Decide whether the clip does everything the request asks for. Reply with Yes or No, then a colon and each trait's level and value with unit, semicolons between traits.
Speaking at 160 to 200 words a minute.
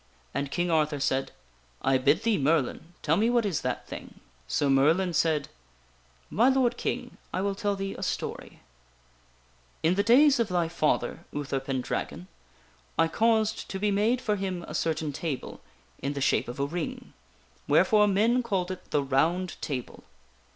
Yes: average, 180 wpm